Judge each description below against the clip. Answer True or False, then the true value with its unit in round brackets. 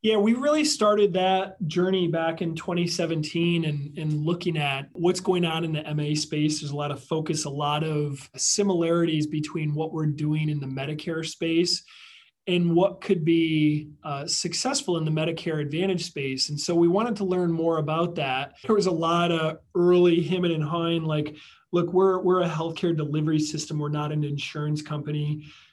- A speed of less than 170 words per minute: False (185 wpm)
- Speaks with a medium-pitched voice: True (165 Hz)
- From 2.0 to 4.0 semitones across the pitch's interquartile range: True (2.7 semitones)